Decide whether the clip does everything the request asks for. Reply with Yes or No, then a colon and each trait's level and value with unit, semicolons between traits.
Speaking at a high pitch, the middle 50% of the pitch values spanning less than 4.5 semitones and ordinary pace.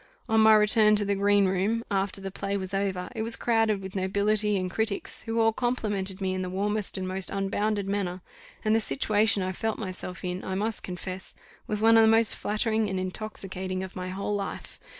No: high, 200 Hz; narrow, 2.4 semitones; fast, 210 wpm